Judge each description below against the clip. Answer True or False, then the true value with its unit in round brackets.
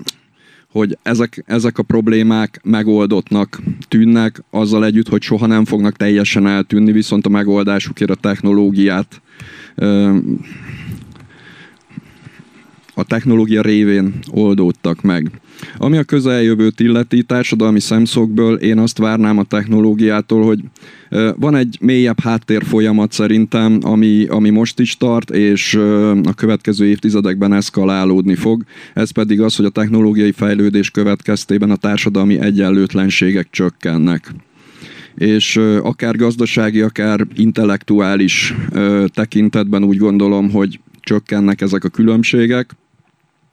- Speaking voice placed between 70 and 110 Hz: True (105 Hz)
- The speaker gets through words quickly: False (110 wpm)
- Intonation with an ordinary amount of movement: False (1.8 semitones)